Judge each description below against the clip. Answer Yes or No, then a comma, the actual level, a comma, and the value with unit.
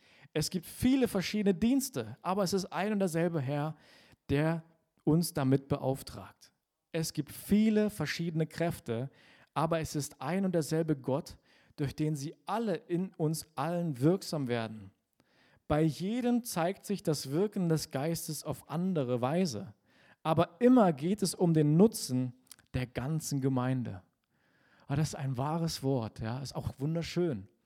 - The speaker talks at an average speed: Yes, average, 150 wpm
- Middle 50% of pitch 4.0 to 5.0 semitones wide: Yes, average, 4.4 semitones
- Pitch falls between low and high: Yes, medium, 155 Hz